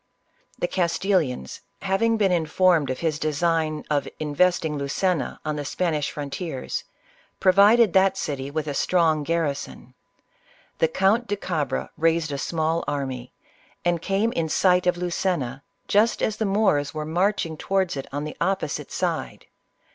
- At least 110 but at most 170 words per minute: Yes, average, 145 wpm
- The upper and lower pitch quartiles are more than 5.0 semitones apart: No, average, 4.2 semitones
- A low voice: No, medium, 165 Hz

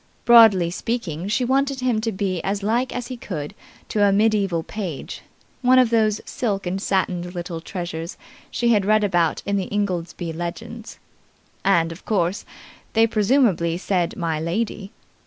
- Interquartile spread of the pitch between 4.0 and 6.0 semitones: Yes, average, 4.5 semitones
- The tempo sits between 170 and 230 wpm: No, average, 155 wpm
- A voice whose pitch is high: Yes, high, 200 Hz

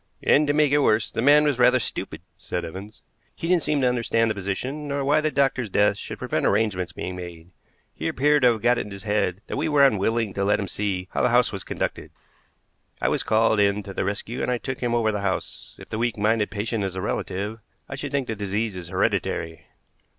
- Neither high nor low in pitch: No, low, 110 Hz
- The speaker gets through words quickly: Yes, fast, 240 wpm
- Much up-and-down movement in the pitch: No, average, 4.7 semitones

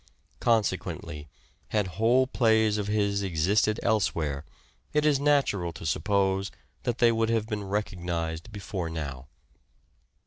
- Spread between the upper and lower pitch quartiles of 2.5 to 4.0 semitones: No, average, 4.6 semitones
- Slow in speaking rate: Yes, slow, 130 wpm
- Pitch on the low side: Yes, low, 105 Hz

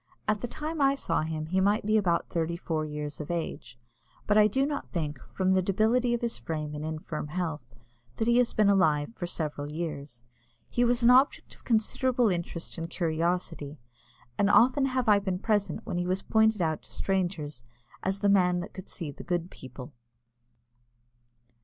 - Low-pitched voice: No, medium, 180 Hz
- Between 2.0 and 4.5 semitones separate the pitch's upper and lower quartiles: No, wide, 5.6 semitones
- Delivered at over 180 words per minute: Yes, average, 190 wpm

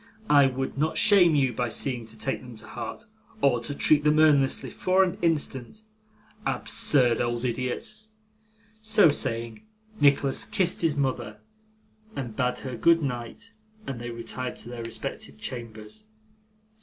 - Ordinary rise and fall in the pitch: Yes, average, 4.8 semitones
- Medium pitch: No, low, 130 Hz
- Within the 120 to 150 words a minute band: Yes, average, 145 wpm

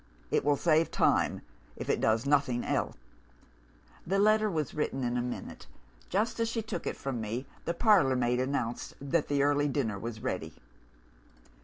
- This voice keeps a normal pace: Yes, average, 170 wpm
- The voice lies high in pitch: No, medium, 140 Hz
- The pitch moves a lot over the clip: Yes, wide, 5.7 semitones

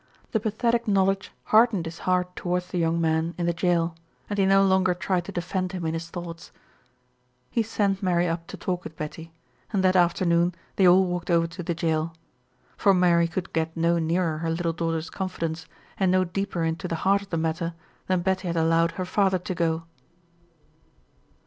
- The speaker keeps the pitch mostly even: Yes, narrow, 2.2 semitones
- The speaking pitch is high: No, medium, 175 Hz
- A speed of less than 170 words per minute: No, average, 195 wpm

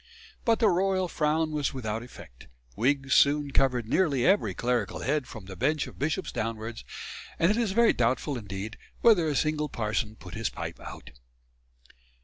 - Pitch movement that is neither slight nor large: No, wide, 5.9 semitones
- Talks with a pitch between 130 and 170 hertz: Yes, medium, 140 Hz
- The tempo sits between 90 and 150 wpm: No, average, 165 wpm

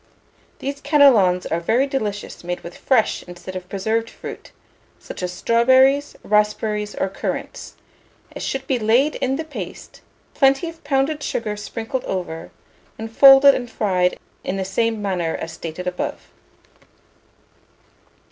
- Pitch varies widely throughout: Yes, wide, 6.4 semitones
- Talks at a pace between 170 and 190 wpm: No, average, 140 wpm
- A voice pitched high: Yes, high, 220 Hz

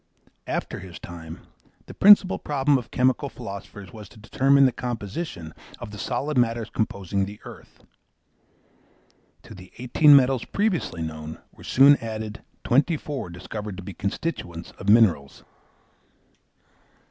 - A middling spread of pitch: No, wide, 6.1 semitones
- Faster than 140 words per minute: No, slow, 135 wpm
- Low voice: Yes, low, 110 Hz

